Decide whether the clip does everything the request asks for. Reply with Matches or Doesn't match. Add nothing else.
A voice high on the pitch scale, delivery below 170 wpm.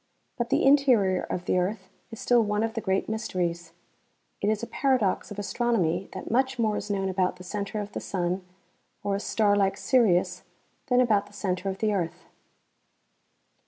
Doesn't match